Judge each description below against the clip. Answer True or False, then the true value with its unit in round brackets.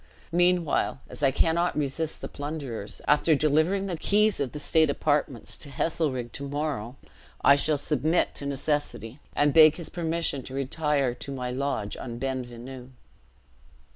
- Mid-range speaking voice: True (145 Hz)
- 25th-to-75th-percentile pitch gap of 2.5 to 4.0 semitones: True (3.1 semitones)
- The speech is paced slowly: False (155 wpm)